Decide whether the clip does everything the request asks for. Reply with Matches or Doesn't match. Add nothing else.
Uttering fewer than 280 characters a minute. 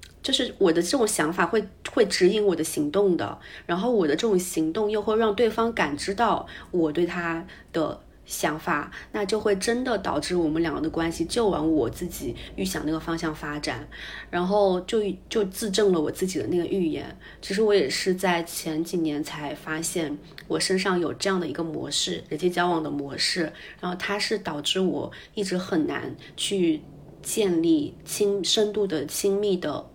Matches